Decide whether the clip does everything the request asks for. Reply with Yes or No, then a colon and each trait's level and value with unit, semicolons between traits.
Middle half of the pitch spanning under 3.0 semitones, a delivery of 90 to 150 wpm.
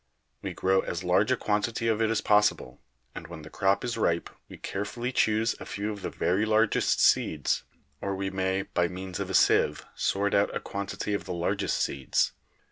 No: narrow, 2.5 semitones; average, 200 wpm